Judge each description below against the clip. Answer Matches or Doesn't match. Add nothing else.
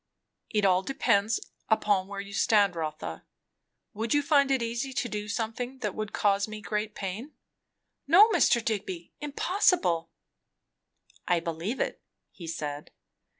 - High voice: Matches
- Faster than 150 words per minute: Doesn't match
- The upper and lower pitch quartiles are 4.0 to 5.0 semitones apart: Matches